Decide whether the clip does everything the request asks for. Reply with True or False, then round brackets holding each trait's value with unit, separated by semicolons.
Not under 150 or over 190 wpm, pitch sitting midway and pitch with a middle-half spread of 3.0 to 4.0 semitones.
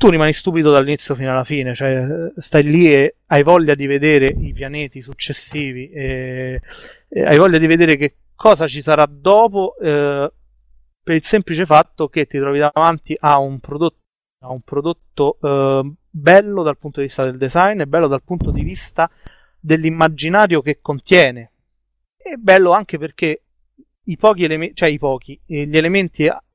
True (160 wpm; 150 Hz; 3.3 semitones)